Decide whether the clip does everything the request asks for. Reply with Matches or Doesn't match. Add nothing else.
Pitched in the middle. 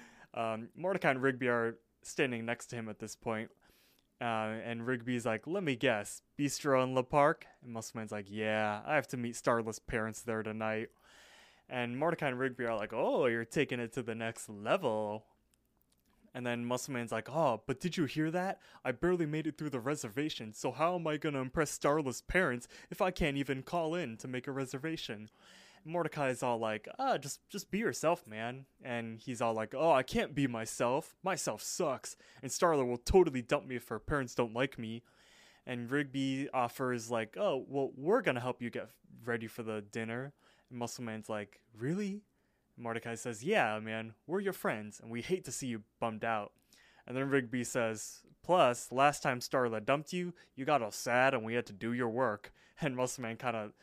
Doesn't match